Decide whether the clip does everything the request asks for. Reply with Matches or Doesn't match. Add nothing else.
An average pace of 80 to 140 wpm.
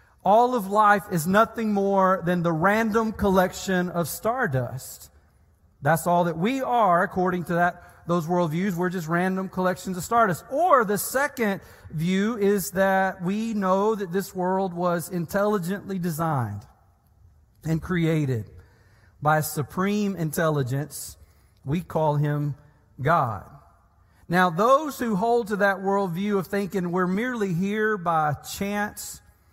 Matches